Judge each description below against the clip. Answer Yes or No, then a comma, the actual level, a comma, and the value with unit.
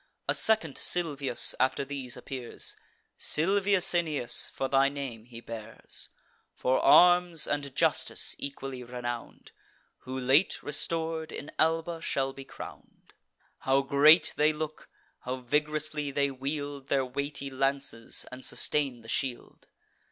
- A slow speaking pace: Yes, slow, 125 wpm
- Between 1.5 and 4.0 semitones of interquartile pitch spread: Yes, average, 3.0 semitones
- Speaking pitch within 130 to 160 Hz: Yes, medium, 140 Hz